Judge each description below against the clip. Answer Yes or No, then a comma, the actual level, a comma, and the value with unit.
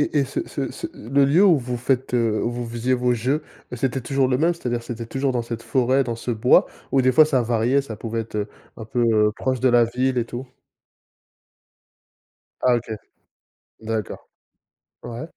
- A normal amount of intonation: No, narrow, 2.3 semitones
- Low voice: Yes, low, 125 Hz